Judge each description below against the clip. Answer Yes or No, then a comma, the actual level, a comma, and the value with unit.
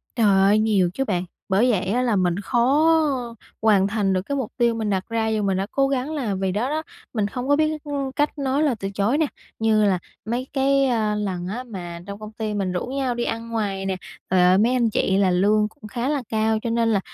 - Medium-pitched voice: No, high, 220 Hz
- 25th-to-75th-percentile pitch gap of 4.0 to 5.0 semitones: Yes, average, 4.5 semitones